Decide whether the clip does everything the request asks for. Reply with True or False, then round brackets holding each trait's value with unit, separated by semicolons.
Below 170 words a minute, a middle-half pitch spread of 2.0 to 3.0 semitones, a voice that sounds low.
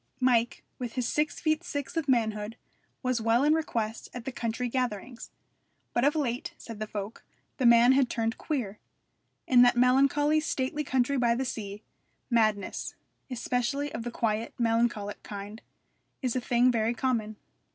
False (160 wpm; 2.7 semitones; 240 Hz)